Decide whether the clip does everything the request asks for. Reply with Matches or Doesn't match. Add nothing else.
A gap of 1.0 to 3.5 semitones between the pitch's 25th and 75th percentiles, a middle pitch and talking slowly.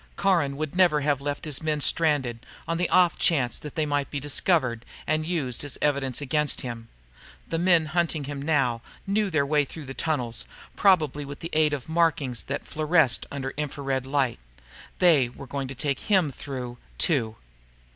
Doesn't match